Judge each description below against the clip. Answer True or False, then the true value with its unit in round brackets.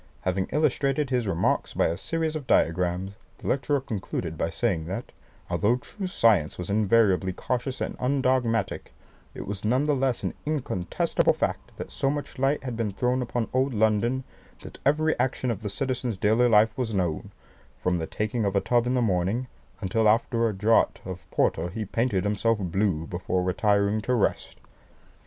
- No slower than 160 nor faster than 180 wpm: True (175 wpm)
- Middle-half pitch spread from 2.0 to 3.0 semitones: False (5.0 semitones)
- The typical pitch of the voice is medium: False (110 Hz)